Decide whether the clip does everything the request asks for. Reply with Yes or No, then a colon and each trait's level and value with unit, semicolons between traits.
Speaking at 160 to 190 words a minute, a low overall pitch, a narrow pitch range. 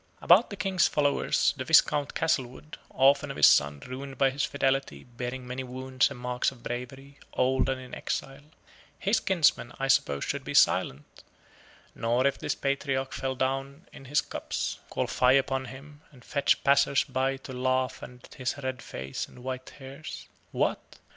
Yes: average, 170 wpm; low, 130 Hz; narrow, 1.7 semitones